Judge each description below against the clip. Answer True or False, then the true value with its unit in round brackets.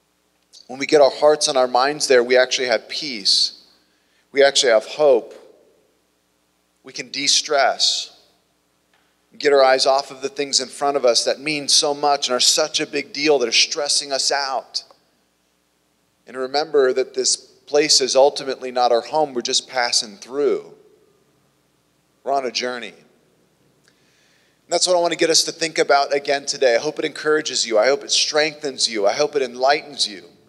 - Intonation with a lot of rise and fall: True (6.7 semitones)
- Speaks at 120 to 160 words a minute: False (185 wpm)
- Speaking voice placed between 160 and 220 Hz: False (135 Hz)